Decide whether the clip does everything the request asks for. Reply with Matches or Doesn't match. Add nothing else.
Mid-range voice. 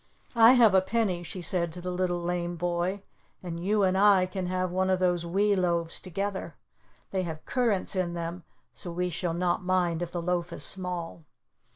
Matches